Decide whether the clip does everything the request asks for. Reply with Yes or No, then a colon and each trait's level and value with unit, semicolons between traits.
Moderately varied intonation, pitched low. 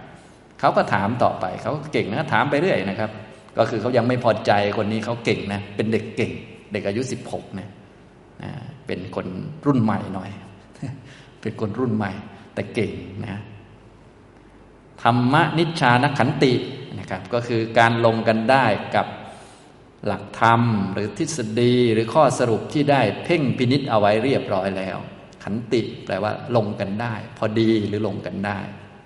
Yes: average, 3.2 semitones; low, 110 Hz